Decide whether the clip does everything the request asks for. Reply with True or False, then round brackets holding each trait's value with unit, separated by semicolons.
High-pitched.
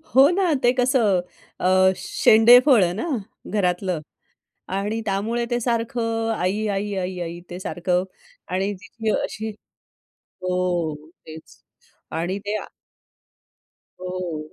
True (195 Hz)